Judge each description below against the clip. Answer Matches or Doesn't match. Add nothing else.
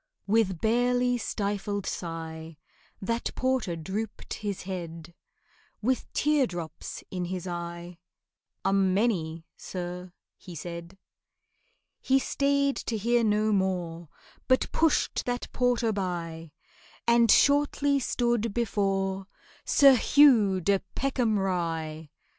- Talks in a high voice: Matches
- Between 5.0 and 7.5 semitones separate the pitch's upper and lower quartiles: Matches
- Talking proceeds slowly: Matches